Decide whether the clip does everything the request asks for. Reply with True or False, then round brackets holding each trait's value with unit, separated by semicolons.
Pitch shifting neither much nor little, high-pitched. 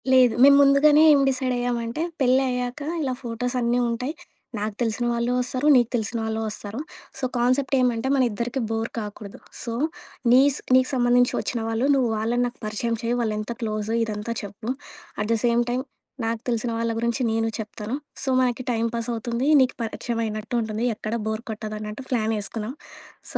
False (2.1 semitones; 235 Hz)